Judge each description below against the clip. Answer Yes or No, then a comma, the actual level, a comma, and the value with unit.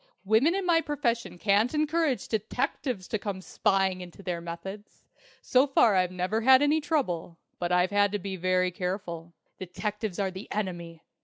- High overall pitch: Yes, high, 200 Hz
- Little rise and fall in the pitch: No, average, 5.3 semitones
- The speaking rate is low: No, average, 165 wpm